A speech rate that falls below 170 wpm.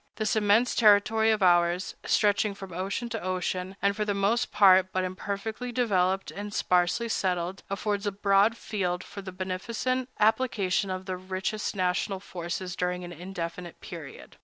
Yes: average, 160 wpm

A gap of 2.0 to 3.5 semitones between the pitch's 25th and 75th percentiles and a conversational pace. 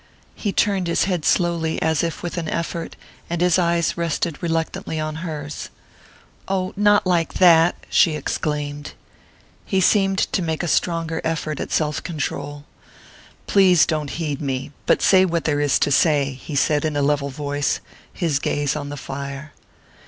Yes: average, 2.9 semitones; average, 165 wpm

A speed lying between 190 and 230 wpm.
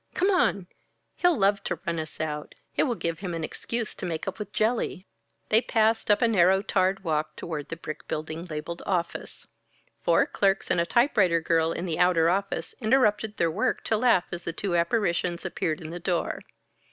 Yes: average, 195 wpm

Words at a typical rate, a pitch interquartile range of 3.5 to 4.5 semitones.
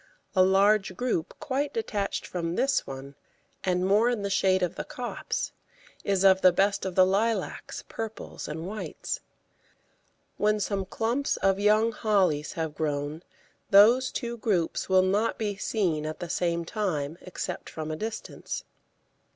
Yes: average, 150 wpm; average, 3.9 semitones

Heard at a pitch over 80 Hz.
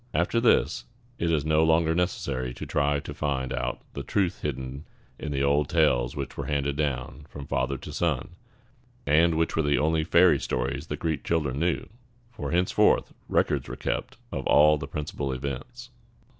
No: very low, 75 Hz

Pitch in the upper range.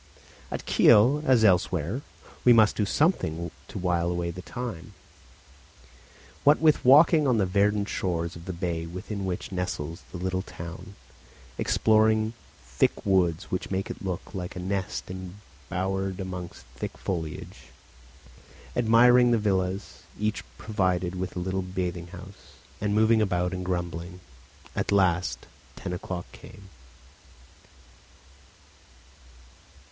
No: very low, 95 Hz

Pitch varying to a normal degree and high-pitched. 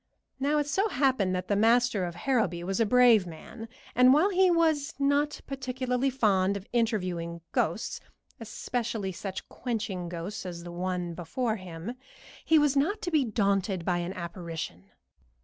No: wide, 6.6 semitones; high, 215 Hz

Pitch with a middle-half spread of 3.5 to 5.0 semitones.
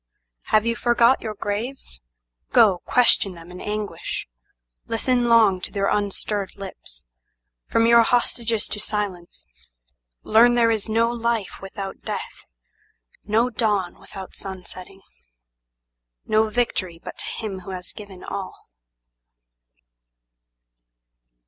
Yes: average, 4.5 semitones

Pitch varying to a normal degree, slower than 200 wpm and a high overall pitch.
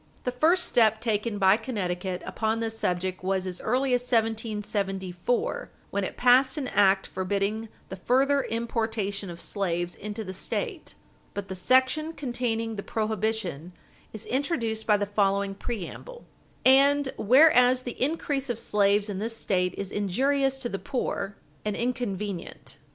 Yes: average, 4.1 semitones; average, 145 wpm; high, 220 Hz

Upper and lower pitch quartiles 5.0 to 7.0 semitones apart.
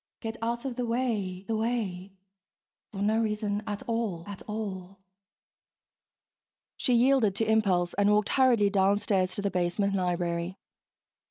No: average, 3.2 semitones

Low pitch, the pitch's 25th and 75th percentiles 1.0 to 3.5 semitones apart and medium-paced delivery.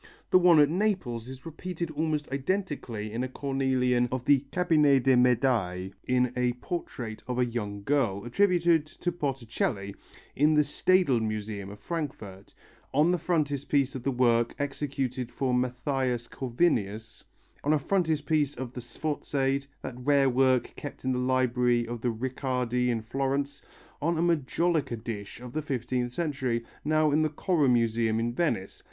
No: low, 130 Hz; average, 3.9 semitones; average, 155 wpm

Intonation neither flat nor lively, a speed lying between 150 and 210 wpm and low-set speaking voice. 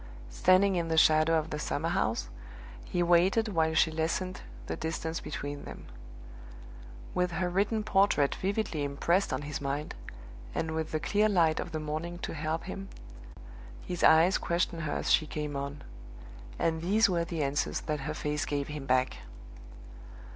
No: average, 3.1 semitones; average, 165 wpm; medium, 160 Hz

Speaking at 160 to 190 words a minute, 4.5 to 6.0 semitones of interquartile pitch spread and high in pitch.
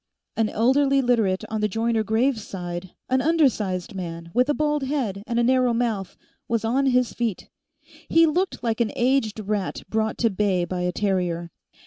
Yes: average, 175 wpm; average, 4.9 semitones; high, 225 Hz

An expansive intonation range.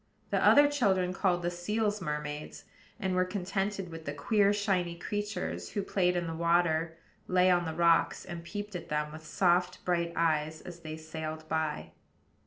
No: average, 3.2 semitones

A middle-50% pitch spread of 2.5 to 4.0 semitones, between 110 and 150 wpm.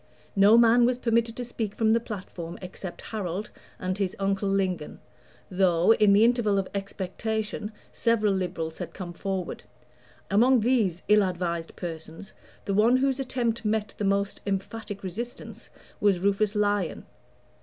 Yes: average, 3.2 semitones; average, 145 wpm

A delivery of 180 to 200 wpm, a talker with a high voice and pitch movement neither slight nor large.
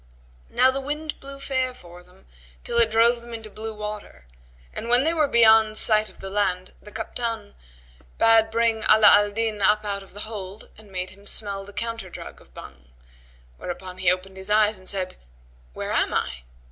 Yes: average, 190 wpm; high, 215 Hz; average, 3.1 semitones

